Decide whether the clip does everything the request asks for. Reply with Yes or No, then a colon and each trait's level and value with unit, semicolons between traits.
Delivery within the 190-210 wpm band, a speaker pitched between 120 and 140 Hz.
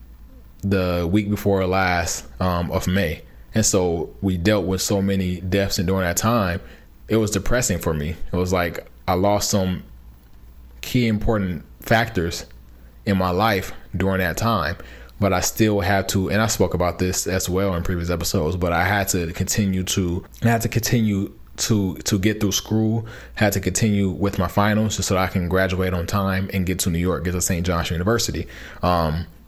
No: average, 195 wpm; very low, 95 Hz